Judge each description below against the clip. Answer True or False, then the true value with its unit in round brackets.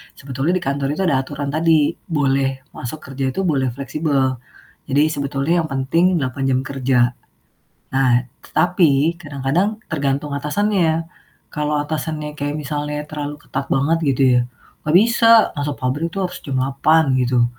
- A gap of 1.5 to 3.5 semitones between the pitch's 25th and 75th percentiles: True (2.9 semitones)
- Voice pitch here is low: False (145 Hz)